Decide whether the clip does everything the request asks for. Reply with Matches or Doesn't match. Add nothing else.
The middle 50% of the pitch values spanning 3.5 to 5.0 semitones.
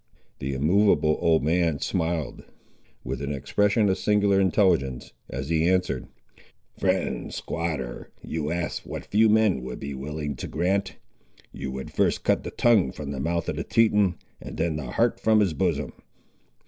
Doesn't match